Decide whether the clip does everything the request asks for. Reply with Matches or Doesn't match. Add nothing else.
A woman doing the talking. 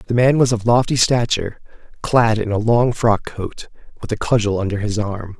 Doesn't match